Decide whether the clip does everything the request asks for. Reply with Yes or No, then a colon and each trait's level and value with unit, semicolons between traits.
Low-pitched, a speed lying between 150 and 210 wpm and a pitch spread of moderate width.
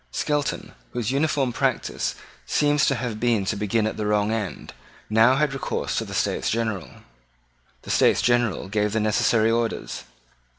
Yes: low, 115 Hz; average, 160 wpm; average, 3.3 semitones